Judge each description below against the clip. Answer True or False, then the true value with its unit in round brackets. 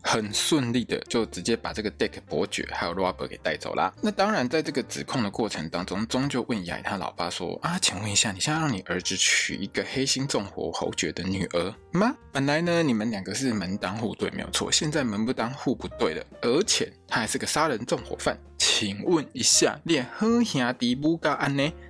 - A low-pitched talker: True (130 Hz)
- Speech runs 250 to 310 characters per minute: False (330 characters per minute)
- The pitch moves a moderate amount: False (8.1 semitones)